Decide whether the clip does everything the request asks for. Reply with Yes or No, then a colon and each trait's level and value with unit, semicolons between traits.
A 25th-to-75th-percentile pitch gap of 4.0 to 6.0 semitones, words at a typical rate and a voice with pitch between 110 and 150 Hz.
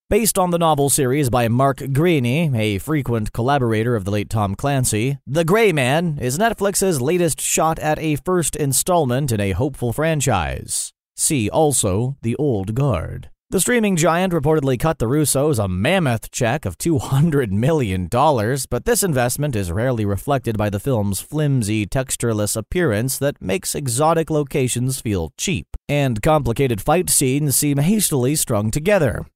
Yes: average, 5.2 semitones; average, 155 wpm; low, 135 Hz